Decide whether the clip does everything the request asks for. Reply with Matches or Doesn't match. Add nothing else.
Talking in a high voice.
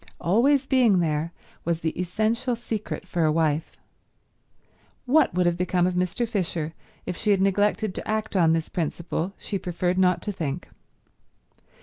Doesn't match